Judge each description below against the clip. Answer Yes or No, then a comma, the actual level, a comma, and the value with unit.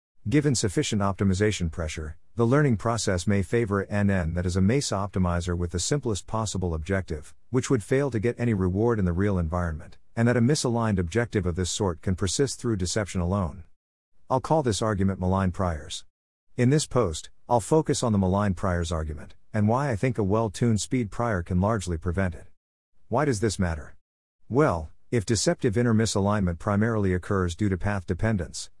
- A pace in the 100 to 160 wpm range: No, average, 185 wpm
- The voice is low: Yes, low, 100 Hz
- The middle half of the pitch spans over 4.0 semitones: Yes, average, 4.6 semitones